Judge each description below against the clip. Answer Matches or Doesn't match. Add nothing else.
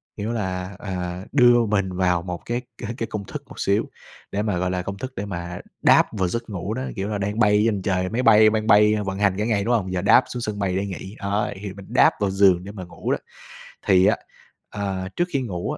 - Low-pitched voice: Matches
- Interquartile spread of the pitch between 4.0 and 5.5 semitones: Doesn't match